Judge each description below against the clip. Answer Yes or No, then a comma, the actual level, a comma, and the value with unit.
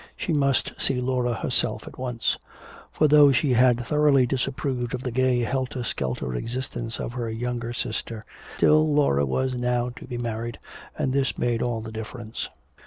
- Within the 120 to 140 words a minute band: No, average, 170 wpm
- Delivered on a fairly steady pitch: Yes, narrow, 2.1 semitones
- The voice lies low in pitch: Yes, low, 125 Hz